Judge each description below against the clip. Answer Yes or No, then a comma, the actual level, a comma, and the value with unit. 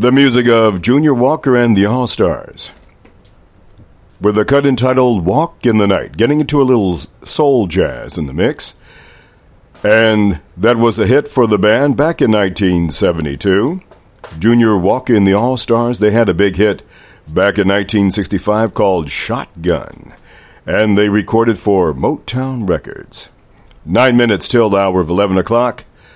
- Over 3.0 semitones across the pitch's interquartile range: Yes, average, 4.0 semitones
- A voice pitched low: Yes, low, 110 Hz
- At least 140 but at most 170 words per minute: Yes, average, 155 wpm